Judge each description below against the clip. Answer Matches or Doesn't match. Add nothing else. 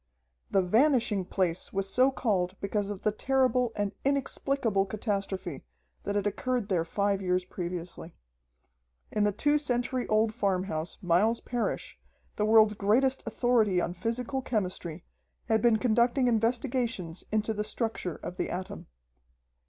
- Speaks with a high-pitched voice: Matches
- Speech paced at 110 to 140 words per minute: Matches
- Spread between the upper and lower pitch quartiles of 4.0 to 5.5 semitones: Matches